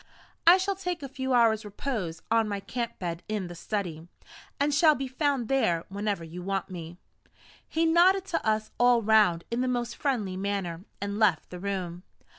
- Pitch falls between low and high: No, high, 215 Hz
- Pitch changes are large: Yes, wide, 6.3 semitones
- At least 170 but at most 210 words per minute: Yes, average, 185 wpm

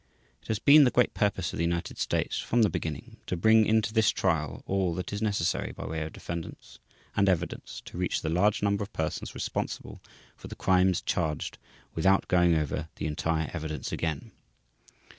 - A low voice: Yes, very low, 90 Hz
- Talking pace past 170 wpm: Yes, average, 190 wpm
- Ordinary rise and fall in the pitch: Yes, average, 4.1 semitones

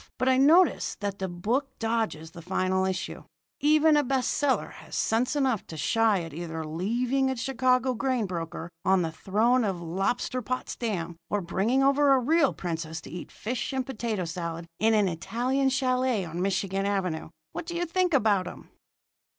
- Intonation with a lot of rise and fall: Yes, wide, 6.5 semitones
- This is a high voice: Yes, high, 220 Hz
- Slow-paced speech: No, average, 175 wpm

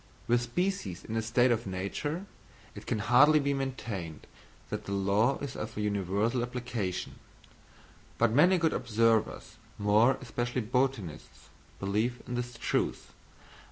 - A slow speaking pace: Yes, slow, 130 wpm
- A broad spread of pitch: No, average, 3.7 semitones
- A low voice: Yes, low, 120 Hz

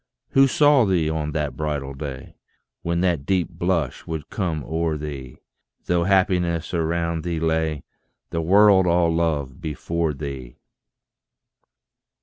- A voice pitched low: Yes, very low, 80 Hz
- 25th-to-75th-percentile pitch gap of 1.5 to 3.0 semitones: Yes, narrow, 2.6 semitones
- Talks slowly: Yes, slow, 130 wpm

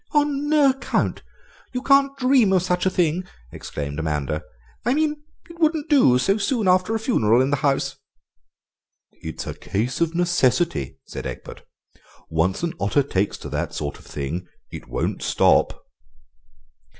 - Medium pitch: Yes, medium, 180 Hz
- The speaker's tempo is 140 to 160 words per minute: Yes, average, 155 wpm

